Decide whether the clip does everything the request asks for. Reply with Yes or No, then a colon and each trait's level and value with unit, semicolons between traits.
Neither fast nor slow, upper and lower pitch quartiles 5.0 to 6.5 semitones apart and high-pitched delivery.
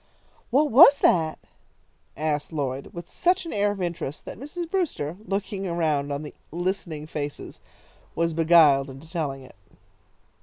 No: average, 145 wpm; wide, 5.4 semitones; medium, 165 Hz